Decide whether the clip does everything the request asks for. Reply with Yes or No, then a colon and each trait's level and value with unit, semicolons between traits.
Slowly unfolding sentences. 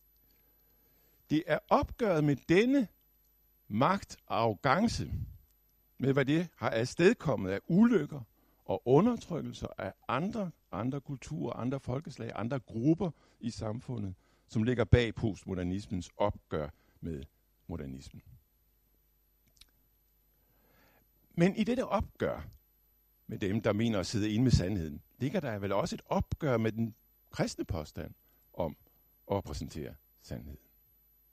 Yes: slow, 115 wpm